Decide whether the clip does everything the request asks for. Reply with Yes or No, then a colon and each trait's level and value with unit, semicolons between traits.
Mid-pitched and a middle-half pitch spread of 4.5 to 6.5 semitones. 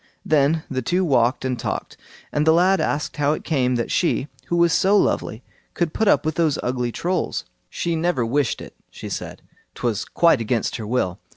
Yes: medium, 145 Hz; wide, 5.5 semitones